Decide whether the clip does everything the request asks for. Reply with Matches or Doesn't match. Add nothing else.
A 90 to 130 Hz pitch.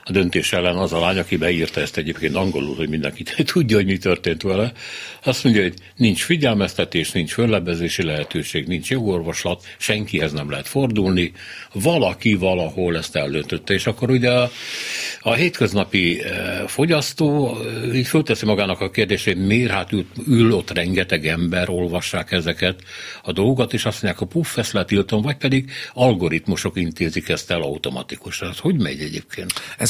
Matches